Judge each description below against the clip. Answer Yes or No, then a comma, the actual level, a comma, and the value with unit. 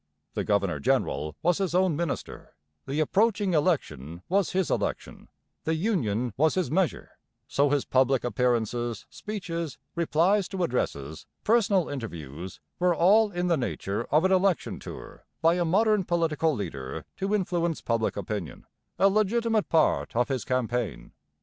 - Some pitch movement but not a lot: No, wide, 8.0 semitones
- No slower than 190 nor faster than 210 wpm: No, average, 145 wpm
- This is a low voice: No, medium, 160 Hz